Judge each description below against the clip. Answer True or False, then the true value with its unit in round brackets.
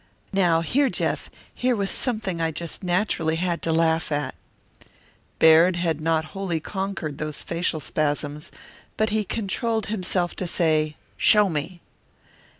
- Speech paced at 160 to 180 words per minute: False (140 wpm)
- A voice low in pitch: False (170 Hz)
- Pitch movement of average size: True (3.6 semitones)